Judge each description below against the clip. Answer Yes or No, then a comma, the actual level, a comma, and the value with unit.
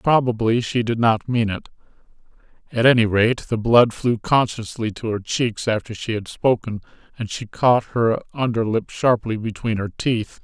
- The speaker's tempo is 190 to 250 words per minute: No, average, 175 wpm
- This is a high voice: No, low, 115 Hz